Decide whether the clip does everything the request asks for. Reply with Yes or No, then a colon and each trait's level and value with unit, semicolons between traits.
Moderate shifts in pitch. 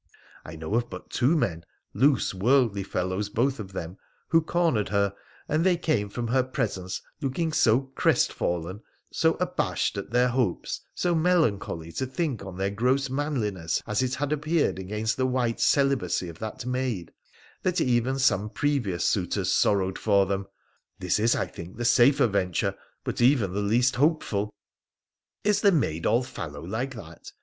No: wide, 5.7 semitones